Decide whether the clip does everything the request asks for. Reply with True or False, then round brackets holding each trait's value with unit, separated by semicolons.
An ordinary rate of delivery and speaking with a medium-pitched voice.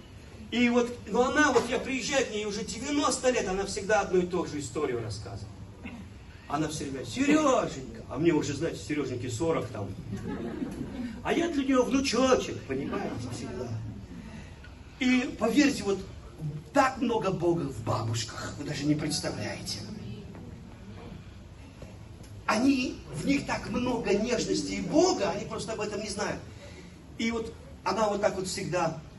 True (150 wpm; 165 Hz)